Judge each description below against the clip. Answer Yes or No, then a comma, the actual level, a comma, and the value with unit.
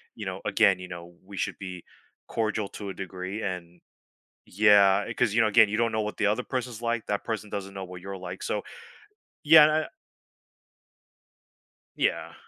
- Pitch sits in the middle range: No, low, 105 Hz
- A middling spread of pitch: Yes, average, 3.0 semitones